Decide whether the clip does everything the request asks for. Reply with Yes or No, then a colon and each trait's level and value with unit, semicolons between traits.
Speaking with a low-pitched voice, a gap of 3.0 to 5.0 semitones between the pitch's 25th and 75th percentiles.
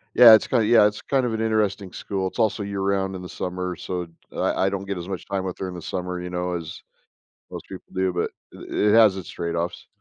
No: very low, 95 Hz; narrow, 2.6 semitones